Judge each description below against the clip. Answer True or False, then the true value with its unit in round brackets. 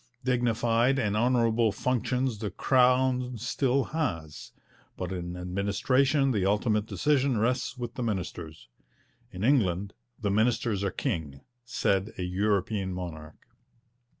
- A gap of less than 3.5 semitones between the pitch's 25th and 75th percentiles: False (4.9 semitones)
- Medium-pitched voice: False (110 Hz)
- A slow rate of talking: True (120 wpm)